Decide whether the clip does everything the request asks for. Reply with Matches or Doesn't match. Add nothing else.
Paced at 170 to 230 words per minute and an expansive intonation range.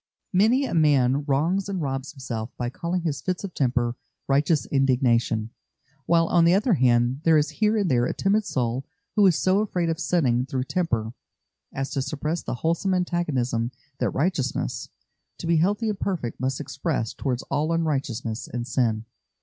Matches